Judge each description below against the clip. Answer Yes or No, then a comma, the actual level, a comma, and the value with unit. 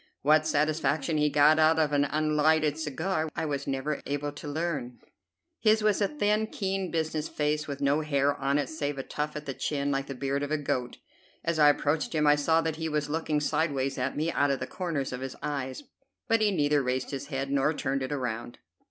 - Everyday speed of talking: No, fast, 220 wpm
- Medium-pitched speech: Yes, medium, 150 Hz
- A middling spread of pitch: No, narrow, 2.2 semitones